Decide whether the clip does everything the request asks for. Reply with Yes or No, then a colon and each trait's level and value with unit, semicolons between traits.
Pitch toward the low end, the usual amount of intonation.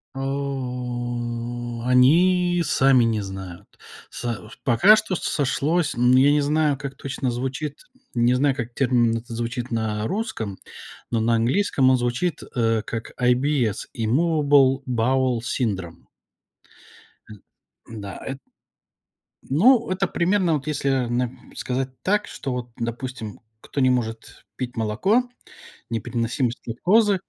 Yes: low, 125 Hz; average, 3.7 semitones